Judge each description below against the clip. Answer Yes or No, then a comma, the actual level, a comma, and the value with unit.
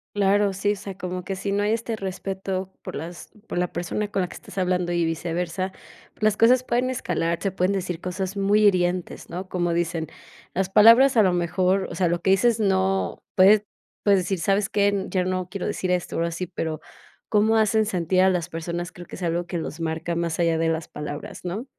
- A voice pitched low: No, medium, 185 Hz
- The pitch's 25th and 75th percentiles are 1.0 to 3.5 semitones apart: Yes, narrow, 2.6 semitones